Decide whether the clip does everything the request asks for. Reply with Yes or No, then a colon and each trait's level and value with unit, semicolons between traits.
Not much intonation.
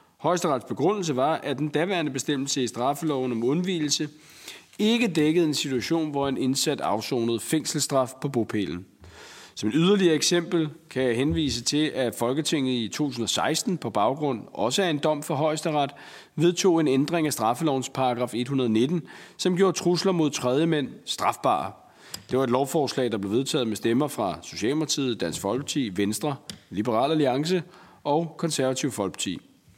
No: average, 4.0 semitones